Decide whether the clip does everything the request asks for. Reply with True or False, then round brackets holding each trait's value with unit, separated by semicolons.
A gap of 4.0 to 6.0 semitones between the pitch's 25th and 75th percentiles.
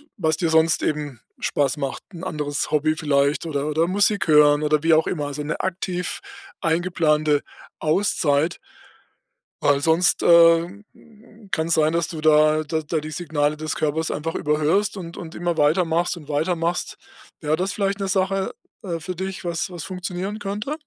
False (2.9 semitones)